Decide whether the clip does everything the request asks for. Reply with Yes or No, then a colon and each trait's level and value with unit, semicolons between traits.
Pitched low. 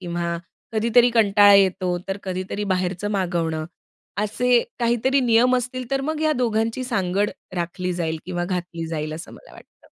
No: high, 200 Hz